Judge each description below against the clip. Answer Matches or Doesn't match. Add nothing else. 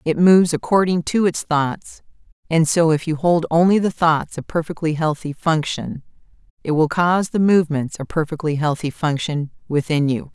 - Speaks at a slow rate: Doesn't match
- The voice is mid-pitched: Matches